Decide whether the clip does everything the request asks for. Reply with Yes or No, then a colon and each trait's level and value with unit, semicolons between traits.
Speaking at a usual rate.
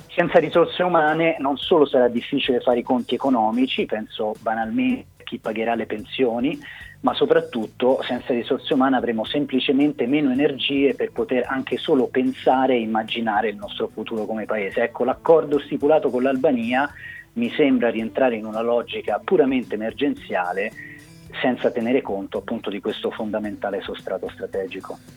Yes: average, 145 wpm